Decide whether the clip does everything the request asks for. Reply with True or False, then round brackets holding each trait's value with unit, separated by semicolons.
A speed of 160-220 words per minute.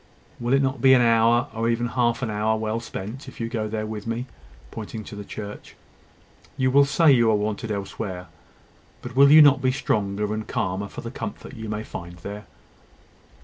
True (200 wpm)